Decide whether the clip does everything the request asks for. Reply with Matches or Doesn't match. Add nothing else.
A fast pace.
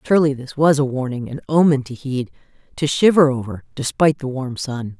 Doesn't match